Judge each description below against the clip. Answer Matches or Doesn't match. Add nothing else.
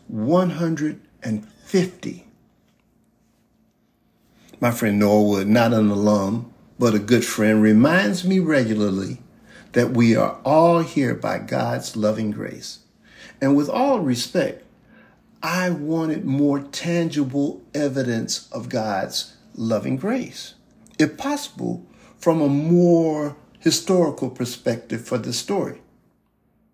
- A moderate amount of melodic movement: Doesn't match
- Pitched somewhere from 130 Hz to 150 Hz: Matches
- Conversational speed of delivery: Doesn't match